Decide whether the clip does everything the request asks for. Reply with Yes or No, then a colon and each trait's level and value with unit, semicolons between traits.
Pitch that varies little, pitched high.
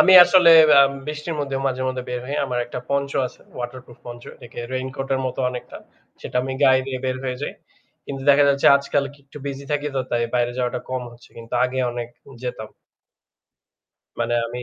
No: narrow, 2.1 semitones; low, 130 Hz